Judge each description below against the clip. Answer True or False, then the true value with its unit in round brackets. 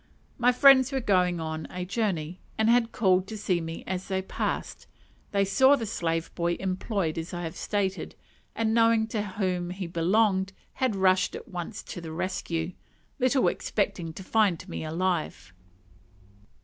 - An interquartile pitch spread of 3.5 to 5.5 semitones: True (4.1 semitones)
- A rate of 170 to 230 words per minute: False (160 wpm)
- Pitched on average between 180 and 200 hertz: True (190 Hz)